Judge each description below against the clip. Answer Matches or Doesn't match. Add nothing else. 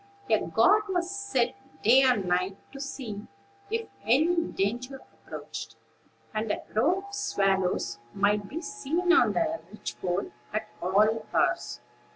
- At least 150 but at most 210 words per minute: Doesn't match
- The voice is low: Doesn't match